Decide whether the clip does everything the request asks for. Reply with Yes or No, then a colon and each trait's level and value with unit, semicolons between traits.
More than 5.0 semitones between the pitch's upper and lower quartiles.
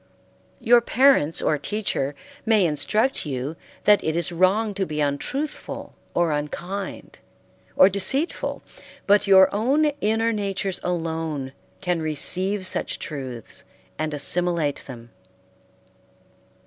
Yes: wide, 5.5 semitones